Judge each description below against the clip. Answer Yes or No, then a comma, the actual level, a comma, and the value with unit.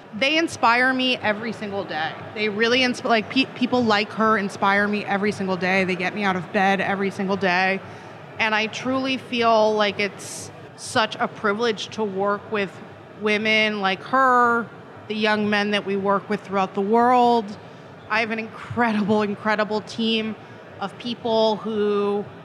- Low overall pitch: No, high, 210 Hz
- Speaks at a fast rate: No, average, 165 wpm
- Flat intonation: Yes, narrow, 2.3 semitones